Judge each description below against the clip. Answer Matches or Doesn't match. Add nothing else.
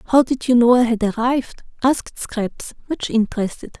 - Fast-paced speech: Doesn't match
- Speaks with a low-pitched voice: Doesn't match